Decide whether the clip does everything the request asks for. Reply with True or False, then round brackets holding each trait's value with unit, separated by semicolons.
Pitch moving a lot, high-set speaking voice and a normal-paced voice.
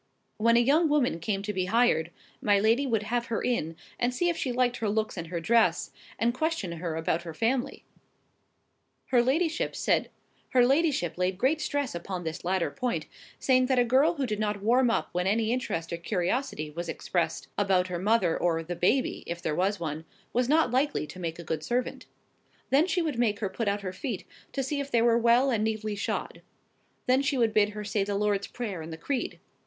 False (5.8 semitones; 220 Hz; 210 wpm)